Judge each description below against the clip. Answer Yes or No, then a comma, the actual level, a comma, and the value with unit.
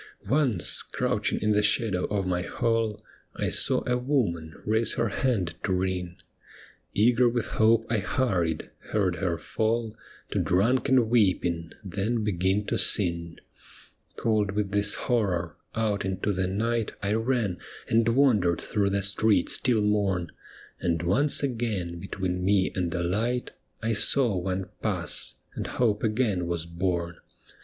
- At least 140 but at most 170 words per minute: Yes, average, 150 wpm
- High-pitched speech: No, low, 100 Hz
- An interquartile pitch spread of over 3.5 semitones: Yes, average, 4.0 semitones